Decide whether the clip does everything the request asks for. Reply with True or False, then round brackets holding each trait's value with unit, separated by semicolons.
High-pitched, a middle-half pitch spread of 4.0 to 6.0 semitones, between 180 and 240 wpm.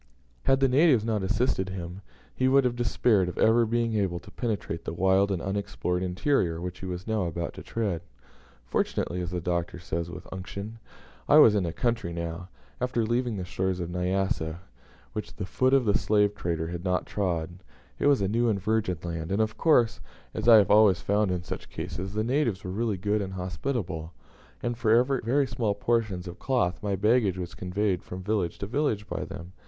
False (100 Hz; 4.3 semitones; 200 wpm)